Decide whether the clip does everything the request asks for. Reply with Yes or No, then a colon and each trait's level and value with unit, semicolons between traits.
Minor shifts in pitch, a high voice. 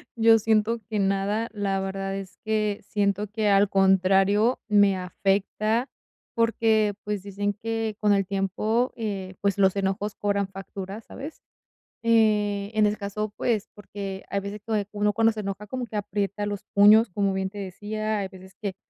Yes: narrow, 1.7 semitones; high, 205 Hz